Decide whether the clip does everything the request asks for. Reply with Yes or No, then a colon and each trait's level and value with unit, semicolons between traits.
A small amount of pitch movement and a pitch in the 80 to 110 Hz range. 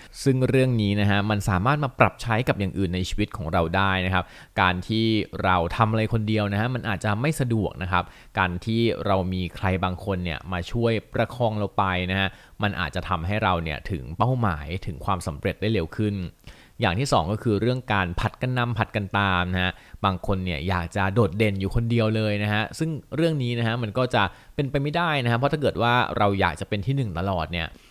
No: average, 4.0 semitones; low, 105 Hz